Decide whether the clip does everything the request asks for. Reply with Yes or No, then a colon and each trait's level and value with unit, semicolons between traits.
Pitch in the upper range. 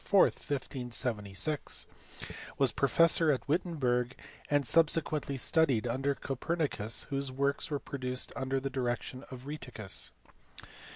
No: low, 135 Hz